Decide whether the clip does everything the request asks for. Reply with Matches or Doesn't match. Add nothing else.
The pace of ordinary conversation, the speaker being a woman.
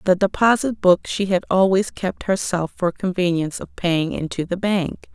Matches